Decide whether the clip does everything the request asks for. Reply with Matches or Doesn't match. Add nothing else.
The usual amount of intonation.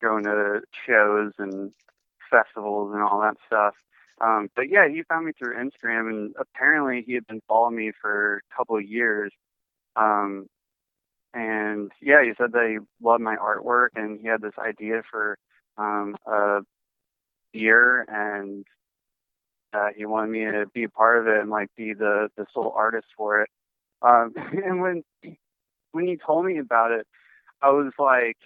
Doesn't match